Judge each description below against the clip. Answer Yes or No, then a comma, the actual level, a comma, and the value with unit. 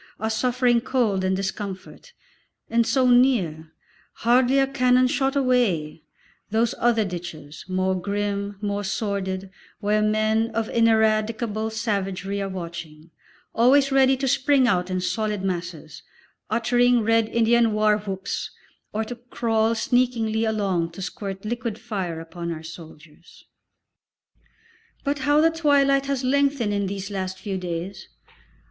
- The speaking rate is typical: No, slow, 130 wpm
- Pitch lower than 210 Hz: No, high, 215 Hz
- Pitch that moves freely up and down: No, average, 4.4 semitones